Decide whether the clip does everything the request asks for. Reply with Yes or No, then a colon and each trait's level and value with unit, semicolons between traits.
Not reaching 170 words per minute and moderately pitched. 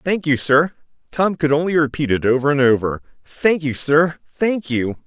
Yes: average, 155 wpm; medium, 150 Hz